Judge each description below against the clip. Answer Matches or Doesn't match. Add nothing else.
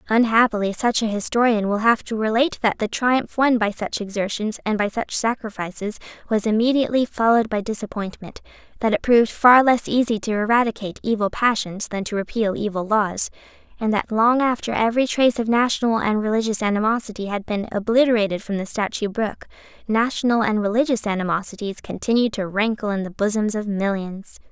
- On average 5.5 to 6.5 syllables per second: Matches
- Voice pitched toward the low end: Doesn't match